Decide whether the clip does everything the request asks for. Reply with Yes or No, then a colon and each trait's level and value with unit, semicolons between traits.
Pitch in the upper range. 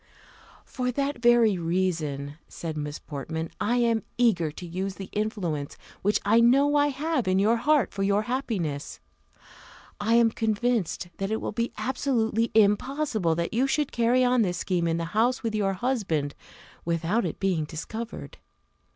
Yes: high, 215 Hz